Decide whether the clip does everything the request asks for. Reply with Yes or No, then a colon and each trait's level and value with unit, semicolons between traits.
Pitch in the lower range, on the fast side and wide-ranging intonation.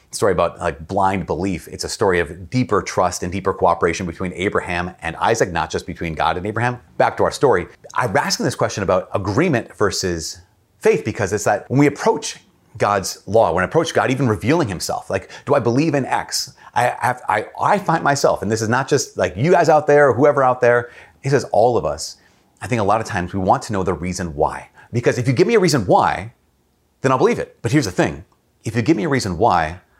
Yes: low, 105 Hz; fast, 240 wpm; wide, 6.0 semitones